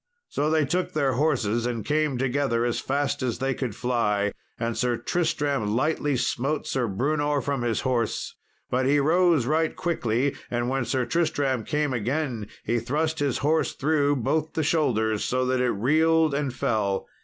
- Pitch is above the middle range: No, low, 135 Hz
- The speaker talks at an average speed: Yes, average, 170 wpm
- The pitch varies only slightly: No, average, 4.0 semitones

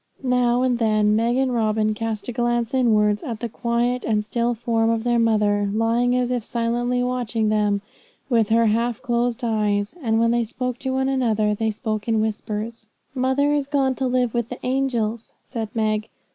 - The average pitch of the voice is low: No, high, 230 Hz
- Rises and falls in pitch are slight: Yes, narrow, 2.3 semitones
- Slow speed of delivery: No, average, 185 wpm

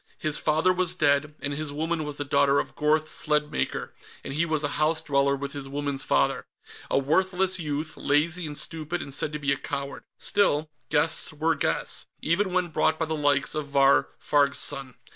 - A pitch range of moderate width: No, narrow, 2.1 semitones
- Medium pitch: Yes, medium, 150 Hz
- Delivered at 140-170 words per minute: No, average, 195 wpm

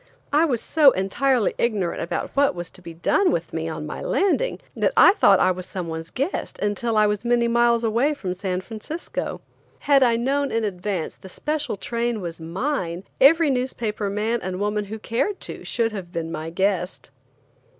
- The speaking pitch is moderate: No, high, 215 Hz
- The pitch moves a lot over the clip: Yes, wide, 5.9 semitones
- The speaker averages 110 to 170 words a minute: No, average, 180 wpm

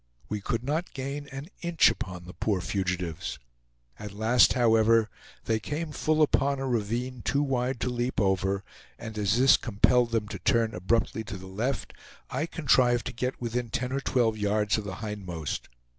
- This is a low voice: Yes, low, 115 Hz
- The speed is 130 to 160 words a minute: No, average, 175 wpm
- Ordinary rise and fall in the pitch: Yes, average, 4.0 semitones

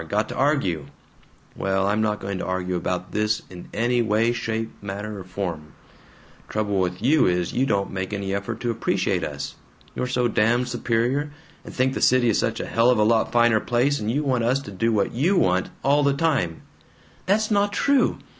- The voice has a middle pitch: No, low, 110 Hz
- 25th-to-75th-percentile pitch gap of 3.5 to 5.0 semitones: Yes, average, 4.5 semitones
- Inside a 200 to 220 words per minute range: Yes, fast, 205 wpm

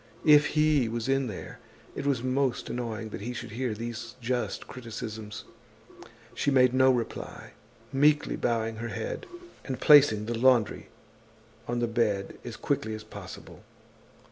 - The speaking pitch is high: No, low, 120 Hz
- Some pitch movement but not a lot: Yes, average, 3.1 semitones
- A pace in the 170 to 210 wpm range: No, average, 145 wpm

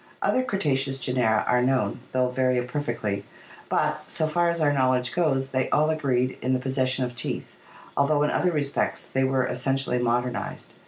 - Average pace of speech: Yes, average, 170 wpm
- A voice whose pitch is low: Yes, low, 130 Hz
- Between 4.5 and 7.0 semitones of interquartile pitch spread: No, narrow, 2.5 semitones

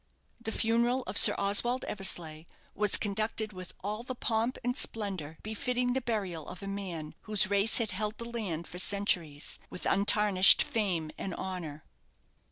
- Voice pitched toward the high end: Yes, high, 200 Hz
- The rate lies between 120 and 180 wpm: Yes, average, 160 wpm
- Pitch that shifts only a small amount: No, average, 3.6 semitones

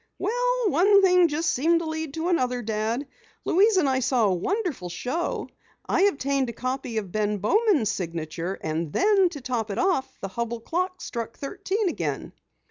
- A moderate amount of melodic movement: No, wide, 8.6 semitones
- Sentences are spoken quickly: No, average, 175 wpm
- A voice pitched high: Yes, very high, 275 Hz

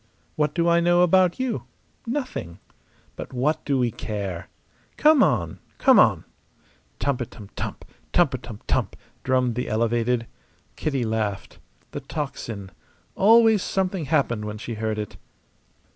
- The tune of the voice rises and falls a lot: Yes, wide, 7.8 semitones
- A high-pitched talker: No, low, 130 Hz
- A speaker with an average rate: No, slow, 130 wpm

